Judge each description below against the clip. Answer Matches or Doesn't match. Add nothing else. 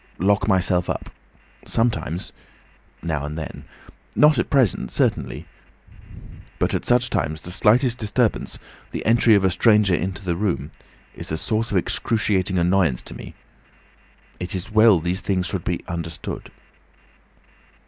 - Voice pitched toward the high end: Doesn't match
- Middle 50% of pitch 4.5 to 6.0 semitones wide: Doesn't match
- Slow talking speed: Matches